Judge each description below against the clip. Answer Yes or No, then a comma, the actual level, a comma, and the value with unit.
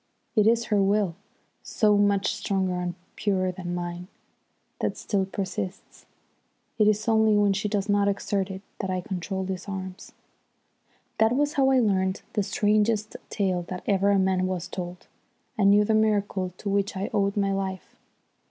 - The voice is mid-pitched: No, high, 200 Hz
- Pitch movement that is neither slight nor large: No, narrow, 1.9 semitones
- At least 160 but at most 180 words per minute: Yes, average, 170 wpm